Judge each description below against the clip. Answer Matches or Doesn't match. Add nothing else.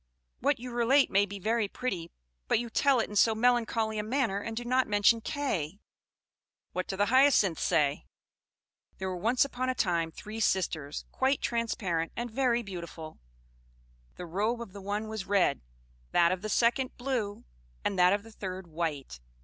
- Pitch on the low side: Doesn't match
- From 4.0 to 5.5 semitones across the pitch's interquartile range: Matches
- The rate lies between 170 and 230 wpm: Matches